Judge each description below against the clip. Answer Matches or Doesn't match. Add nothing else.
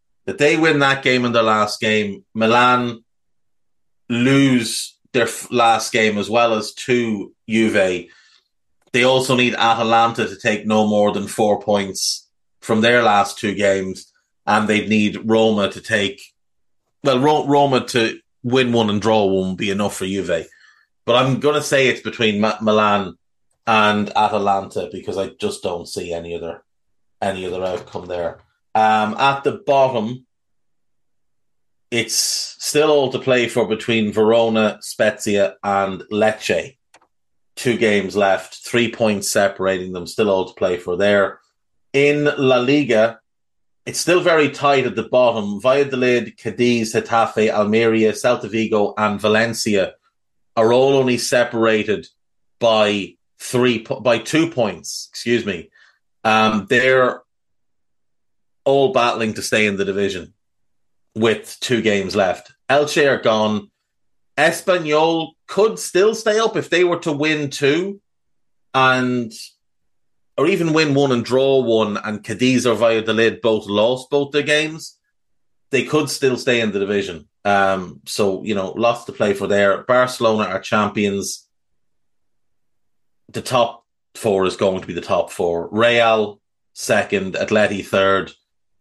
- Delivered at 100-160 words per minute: Matches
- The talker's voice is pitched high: Doesn't match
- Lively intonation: Doesn't match